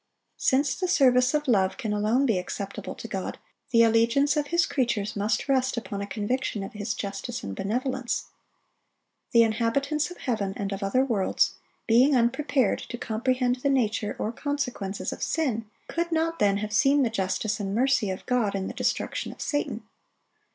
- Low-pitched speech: No, high, 235 Hz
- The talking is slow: No, average, 175 wpm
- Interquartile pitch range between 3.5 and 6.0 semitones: Yes, average, 4.6 semitones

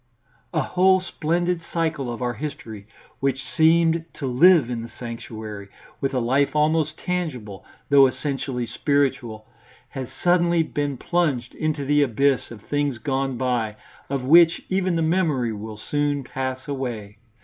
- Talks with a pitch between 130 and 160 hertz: Yes, medium, 140 Hz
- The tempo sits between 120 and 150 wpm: Yes, average, 145 wpm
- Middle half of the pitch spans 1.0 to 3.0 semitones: No, average, 4.8 semitones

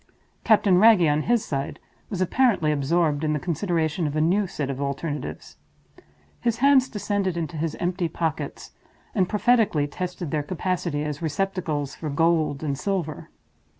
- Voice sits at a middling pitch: Yes, medium, 165 Hz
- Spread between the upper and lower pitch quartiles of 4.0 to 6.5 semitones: Yes, average, 4.5 semitones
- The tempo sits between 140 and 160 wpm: Yes, average, 150 wpm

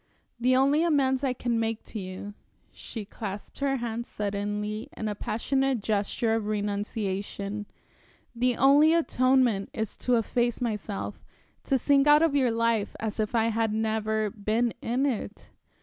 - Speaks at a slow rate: No, average, 150 wpm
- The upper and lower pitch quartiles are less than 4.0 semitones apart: Yes, average, 3.5 semitones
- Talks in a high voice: Yes, high, 225 Hz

